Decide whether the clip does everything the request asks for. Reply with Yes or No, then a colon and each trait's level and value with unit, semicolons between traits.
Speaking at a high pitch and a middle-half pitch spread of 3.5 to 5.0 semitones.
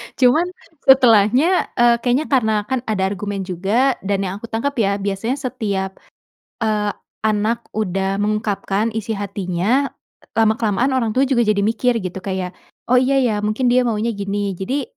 Yes: high, 215 Hz; average, 3.8 semitones